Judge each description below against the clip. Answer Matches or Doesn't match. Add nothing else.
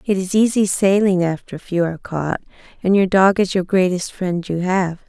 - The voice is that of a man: Doesn't match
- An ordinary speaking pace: Doesn't match